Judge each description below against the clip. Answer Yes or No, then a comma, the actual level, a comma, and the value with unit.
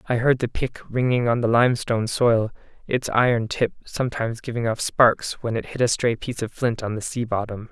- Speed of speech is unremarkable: No, fast, 220 wpm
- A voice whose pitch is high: No, low, 115 Hz